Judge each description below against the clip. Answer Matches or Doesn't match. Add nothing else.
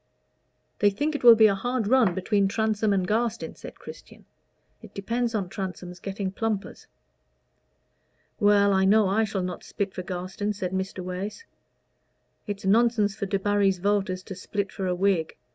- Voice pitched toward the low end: Doesn't match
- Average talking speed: Matches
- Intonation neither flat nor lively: Doesn't match